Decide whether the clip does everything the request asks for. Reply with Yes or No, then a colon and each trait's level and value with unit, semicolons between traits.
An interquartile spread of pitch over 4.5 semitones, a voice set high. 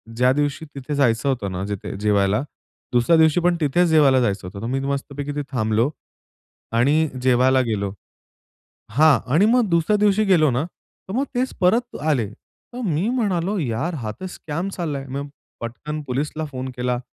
No: wide, 5.6 semitones; medium, 145 Hz